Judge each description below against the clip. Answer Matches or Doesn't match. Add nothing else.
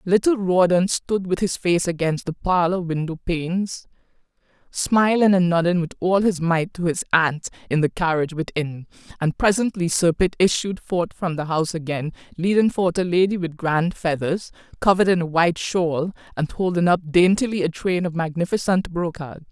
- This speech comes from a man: Doesn't match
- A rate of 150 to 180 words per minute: Matches